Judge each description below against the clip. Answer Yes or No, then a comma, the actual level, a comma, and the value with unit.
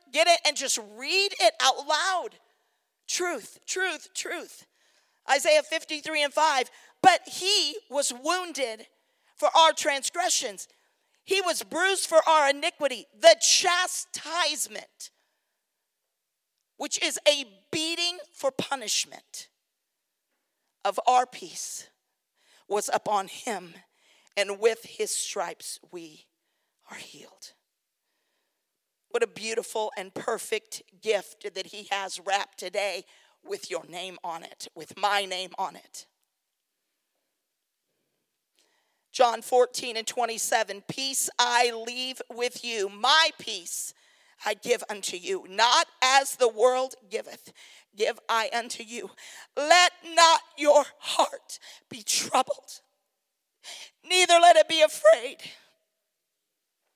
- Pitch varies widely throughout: Yes, wide, 6.8 semitones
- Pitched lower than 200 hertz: No, very high, 275 Hz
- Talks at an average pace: No, slow, 110 wpm